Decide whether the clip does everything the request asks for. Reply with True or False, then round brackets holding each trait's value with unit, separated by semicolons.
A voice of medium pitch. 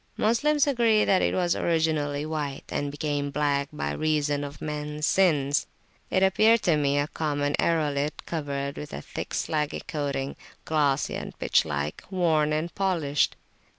True (150 Hz)